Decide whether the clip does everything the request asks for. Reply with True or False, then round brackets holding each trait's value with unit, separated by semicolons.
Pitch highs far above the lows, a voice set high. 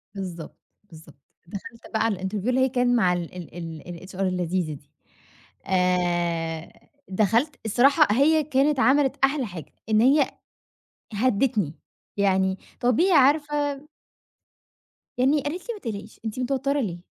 True (6.9 semitones; 225 Hz)